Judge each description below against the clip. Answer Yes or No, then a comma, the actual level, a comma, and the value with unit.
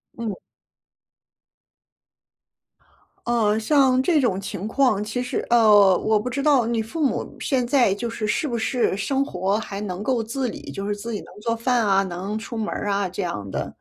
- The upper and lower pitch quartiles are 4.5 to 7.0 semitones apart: No, average, 3.6 semitones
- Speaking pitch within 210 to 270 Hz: Yes, high, 220 Hz